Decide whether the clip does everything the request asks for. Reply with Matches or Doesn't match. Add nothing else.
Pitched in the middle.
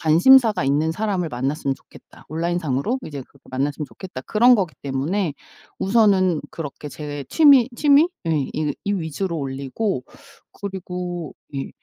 Matches